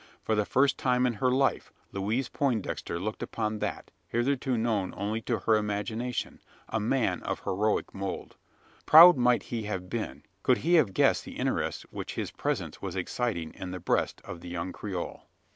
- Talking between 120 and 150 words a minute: No, average, 175 wpm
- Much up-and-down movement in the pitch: No, average, 4.2 semitones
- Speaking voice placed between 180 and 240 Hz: No, low, 110 Hz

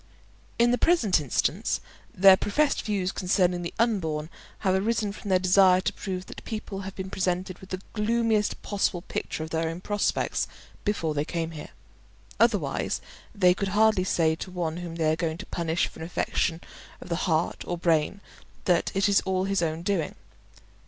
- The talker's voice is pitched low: No, medium, 185 Hz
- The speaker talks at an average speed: Yes, average, 180 wpm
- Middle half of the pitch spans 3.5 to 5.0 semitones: No, average, 3.1 semitones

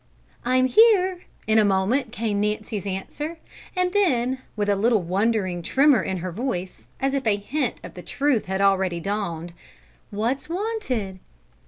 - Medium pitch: No, high, 220 Hz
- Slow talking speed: No, average, 155 wpm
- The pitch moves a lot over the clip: Yes, wide, 6.0 semitones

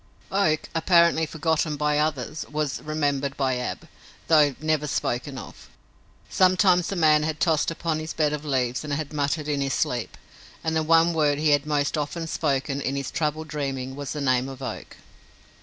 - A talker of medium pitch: Yes, medium, 150 Hz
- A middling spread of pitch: No, narrow, 2.2 semitones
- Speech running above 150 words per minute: Yes, average, 180 wpm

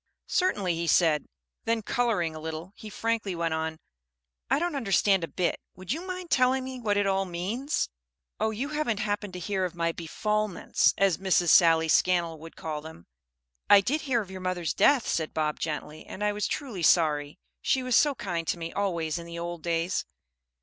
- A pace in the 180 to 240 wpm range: Yes, average, 195 wpm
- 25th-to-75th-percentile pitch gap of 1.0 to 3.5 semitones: No, wide, 5.4 semitones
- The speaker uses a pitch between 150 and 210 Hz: Yes, medium, 185 Hz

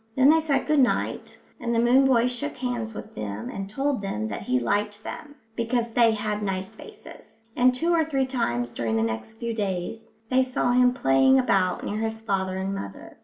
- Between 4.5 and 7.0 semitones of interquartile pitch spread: Yes, average, 5.1 semitones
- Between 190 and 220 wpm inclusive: Yes, fast, 205 wpm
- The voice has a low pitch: No, high, 225 Hz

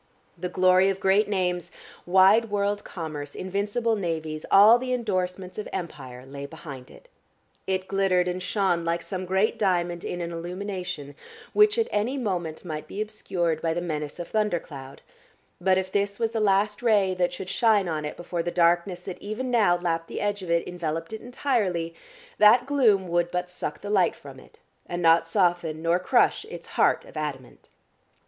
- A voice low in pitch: No, medium, 185 Hz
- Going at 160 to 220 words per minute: Yes, average, 180 wpm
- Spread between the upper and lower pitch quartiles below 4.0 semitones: Yes, average, 3.4 semitones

